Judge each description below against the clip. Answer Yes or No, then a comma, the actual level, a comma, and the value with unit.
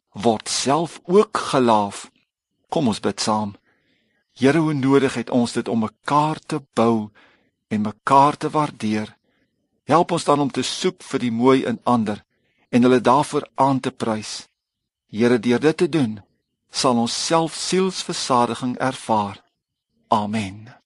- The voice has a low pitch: Yes, low, 125 Hz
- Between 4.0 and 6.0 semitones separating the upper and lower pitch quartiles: Yes, average, 4.6 semitones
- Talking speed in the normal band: Yes, average, 145 wpm